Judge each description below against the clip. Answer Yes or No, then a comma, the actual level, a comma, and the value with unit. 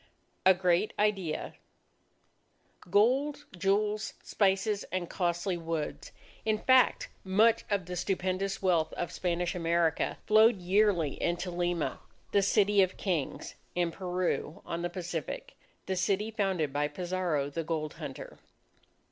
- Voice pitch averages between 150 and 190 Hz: Yes, medium, 185 Hz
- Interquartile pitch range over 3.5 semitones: No, average, 3.0 semitones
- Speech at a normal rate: No, slow, 130 wpm